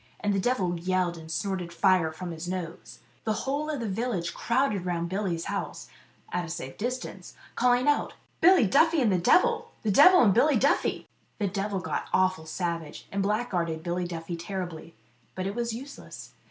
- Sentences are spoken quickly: No, average, 180 wpm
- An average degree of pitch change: No, wide, 6.0 semitones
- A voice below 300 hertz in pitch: Yes, high, 190 Hz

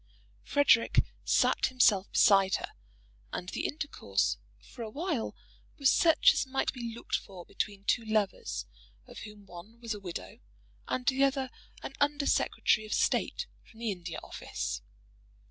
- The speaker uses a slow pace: No, average, 145 wpm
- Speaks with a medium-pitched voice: No, high, 225 Hz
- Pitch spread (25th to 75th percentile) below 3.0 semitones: No, average, 5.2 semitones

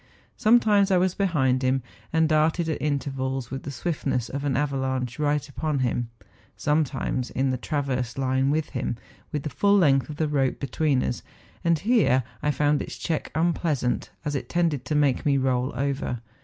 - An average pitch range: Yes, average, 3.1 semitones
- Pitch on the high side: No, medium, 140 Hz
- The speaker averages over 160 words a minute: Yes, average, 180 wpm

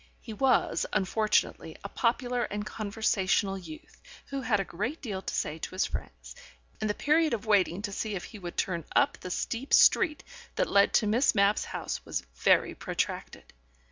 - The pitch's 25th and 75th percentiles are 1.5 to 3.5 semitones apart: No, average, 4.2 semitones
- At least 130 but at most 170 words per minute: No, average, 185 wpm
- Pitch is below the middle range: No, high, 210 Hz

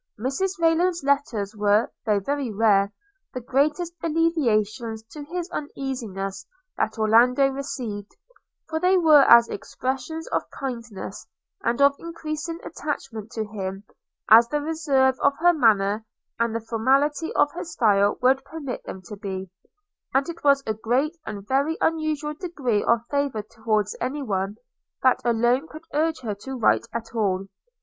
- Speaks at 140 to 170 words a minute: Yes, average, 150 wpm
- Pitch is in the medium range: No, very high, 255 Hz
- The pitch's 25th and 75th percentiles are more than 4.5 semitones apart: Yes, wide, 5.6 semitones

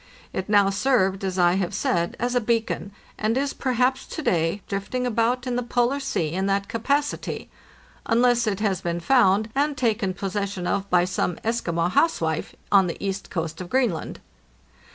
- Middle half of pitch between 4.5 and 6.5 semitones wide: Yes, average, 4.8 semitones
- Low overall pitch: No, high, 205 Hz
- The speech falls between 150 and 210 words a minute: Yes, average, 175 wpm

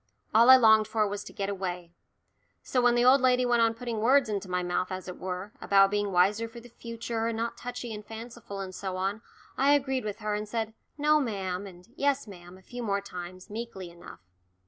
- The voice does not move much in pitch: No, average, 3.8 semitones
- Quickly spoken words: Yes, fast, 220 wpm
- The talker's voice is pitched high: Yes, high, 215 Hz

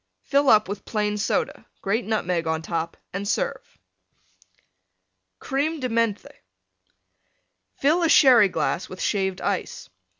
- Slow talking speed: Yes, slow, 125 wpm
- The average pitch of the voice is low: No, high, 210 Hz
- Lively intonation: Yes, wide, 5.9 semitones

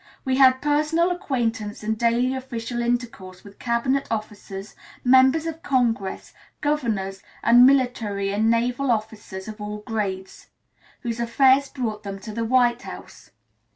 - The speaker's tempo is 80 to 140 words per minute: Yes, slow, 135 wpm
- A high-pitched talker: Yes, high, 235 Hz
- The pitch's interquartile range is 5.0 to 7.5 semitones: No, average, 3.6 semitones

